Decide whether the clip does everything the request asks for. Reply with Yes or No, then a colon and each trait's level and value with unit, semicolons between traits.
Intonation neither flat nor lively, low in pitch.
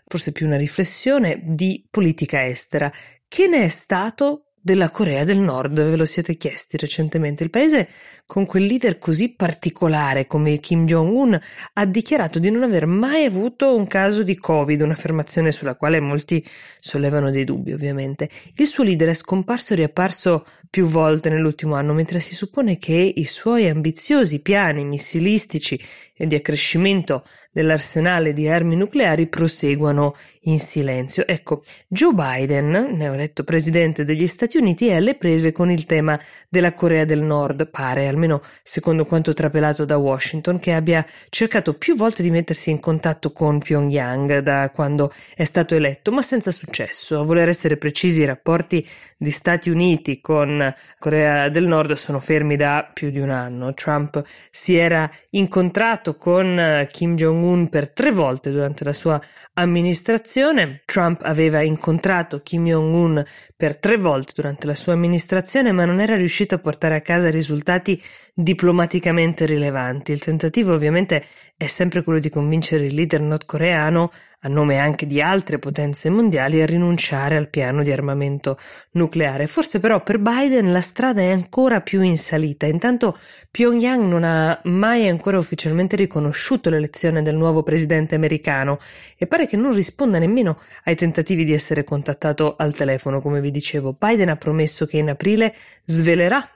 No: average, 3.5 semitones; medium, 165 Hz